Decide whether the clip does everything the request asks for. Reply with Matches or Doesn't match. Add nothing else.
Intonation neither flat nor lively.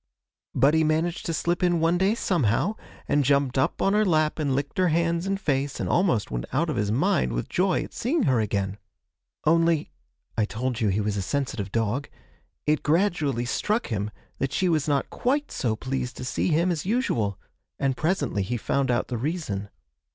Doesn't match